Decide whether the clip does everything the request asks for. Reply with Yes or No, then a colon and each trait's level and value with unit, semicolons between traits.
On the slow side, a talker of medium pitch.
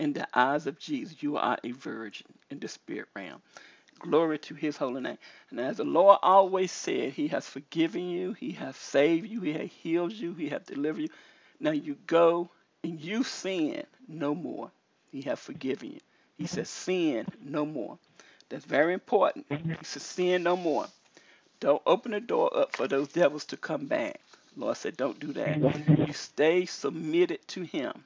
No: average, 185 wpm; medium, 180 Hz